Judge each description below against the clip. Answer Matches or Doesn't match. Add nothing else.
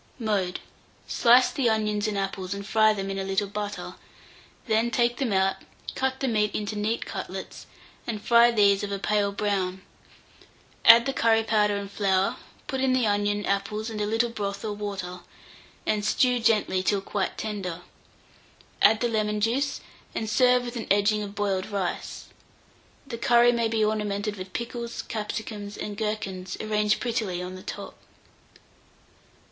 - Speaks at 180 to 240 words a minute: Doesn't match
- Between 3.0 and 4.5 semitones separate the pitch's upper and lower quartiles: Doesn't match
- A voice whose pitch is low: Doesn't match